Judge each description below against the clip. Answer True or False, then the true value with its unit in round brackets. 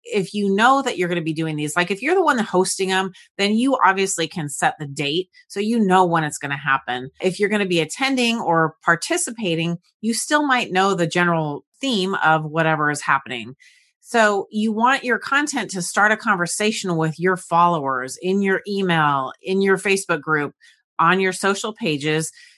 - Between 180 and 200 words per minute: True (195 wpm)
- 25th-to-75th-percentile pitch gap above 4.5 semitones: True (5.2 semitones)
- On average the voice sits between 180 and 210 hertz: True (185 Hz)